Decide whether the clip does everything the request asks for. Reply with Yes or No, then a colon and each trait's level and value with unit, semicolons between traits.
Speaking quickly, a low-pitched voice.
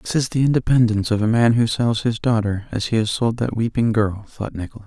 Yes: fast, 260 wpm; low, 115 Hz